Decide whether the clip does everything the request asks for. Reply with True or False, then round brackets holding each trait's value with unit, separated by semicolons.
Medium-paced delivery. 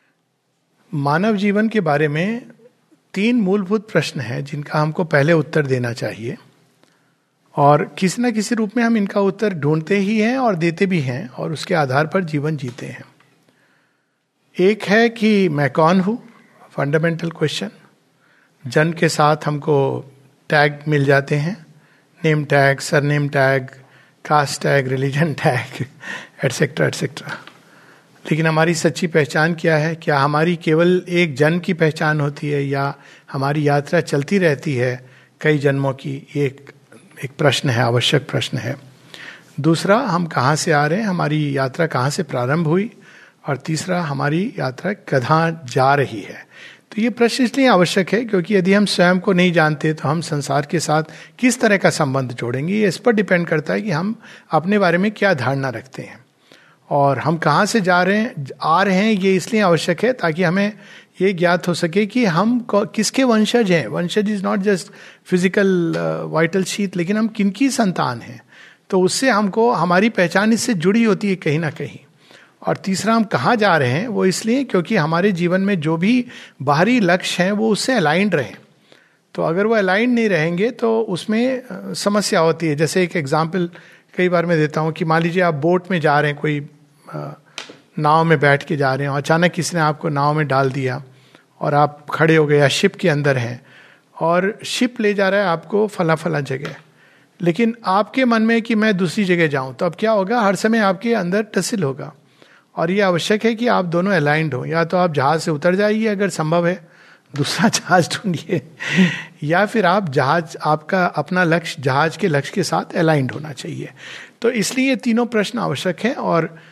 True (180 wpm)